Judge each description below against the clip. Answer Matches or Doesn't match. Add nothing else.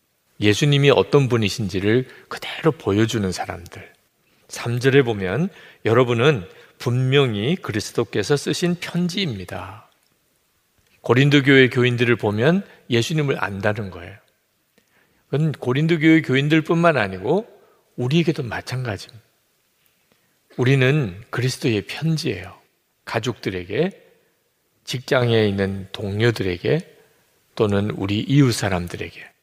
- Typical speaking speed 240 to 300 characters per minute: Matches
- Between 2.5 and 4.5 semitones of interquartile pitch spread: Doesn't match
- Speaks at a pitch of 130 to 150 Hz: Doesn't match